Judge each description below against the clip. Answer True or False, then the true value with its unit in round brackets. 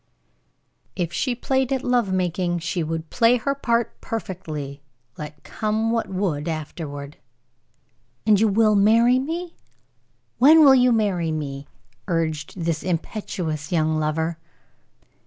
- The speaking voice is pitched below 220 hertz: True (185 Hz)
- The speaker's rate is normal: False (125 wpm)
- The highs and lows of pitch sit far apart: True (6.6 semitones)